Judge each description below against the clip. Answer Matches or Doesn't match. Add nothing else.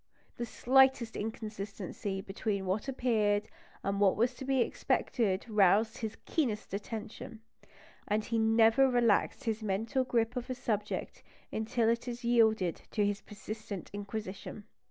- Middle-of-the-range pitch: Doesn't match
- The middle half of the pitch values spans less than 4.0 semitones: Matches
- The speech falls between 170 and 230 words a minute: Doesn't match